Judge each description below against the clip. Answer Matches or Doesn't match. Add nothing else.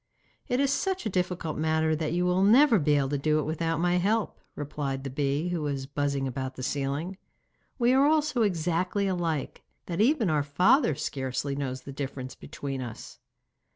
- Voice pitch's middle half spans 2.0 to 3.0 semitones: Doesn't match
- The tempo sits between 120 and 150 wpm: Doesn't match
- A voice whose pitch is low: Doesn't match